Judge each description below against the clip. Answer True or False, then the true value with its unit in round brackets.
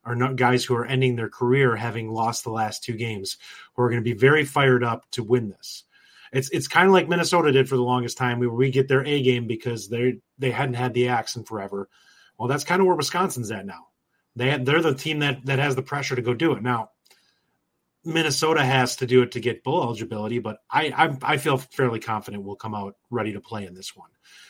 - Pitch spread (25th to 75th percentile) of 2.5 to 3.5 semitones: True (2.9 semitones)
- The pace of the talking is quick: True (240 wpm)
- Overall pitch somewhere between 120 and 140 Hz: True (125 Hz)